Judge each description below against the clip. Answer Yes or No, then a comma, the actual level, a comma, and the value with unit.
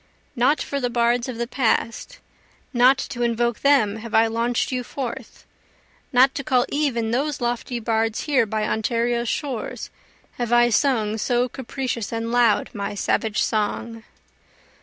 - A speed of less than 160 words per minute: Yes, average, 150 wpm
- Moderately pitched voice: No, high, 240 Hz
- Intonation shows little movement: Yes, narrow, 2.1 semitones